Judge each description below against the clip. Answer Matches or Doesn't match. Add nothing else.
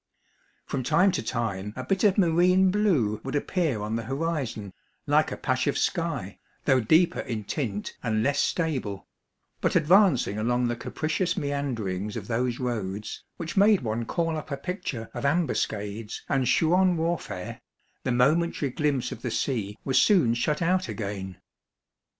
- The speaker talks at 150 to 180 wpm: Matches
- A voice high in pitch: Doesn't match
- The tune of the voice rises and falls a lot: Matches